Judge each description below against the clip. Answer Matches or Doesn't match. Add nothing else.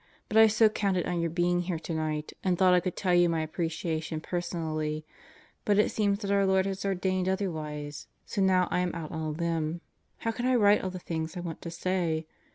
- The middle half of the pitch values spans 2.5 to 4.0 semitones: Matches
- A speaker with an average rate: Doesn't match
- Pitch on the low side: Doesn't match